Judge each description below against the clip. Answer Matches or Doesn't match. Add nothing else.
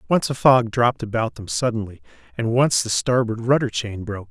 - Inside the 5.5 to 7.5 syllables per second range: Matches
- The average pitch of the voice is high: Doesn't match